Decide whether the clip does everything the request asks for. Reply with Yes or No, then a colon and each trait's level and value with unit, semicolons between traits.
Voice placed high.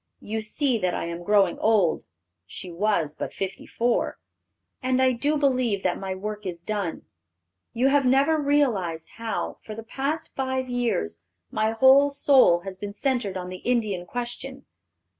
Yes: high, 225 Hz